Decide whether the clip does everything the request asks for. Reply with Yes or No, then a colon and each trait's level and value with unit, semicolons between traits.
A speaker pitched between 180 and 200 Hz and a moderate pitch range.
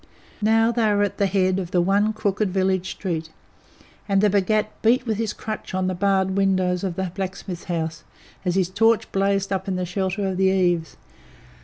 No: high, 190 Hz; narrow, 1.9 semitones